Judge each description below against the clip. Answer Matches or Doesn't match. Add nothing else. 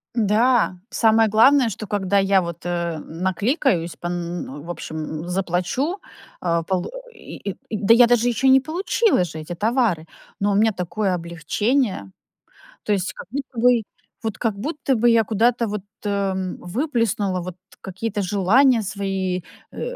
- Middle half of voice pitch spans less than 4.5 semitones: Doesn't match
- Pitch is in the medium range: Doesn't match